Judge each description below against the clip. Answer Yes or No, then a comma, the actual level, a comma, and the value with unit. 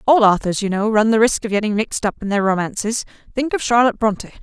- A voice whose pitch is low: No, high, 215 Hz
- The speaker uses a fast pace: Yes, fast, 230 wpm